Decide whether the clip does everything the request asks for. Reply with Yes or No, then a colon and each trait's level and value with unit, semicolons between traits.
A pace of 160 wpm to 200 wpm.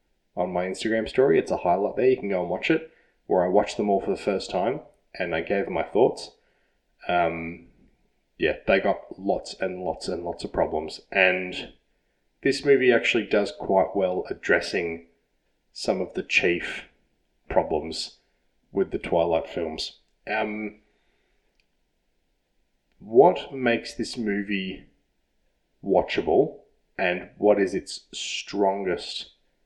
No: average, 140 wpm